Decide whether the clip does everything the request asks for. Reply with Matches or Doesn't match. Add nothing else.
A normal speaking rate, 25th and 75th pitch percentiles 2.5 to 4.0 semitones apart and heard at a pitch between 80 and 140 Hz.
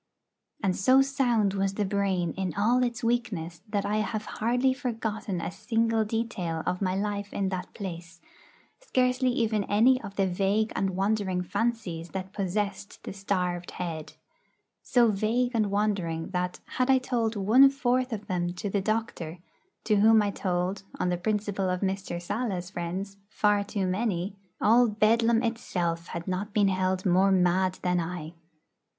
Doesn't match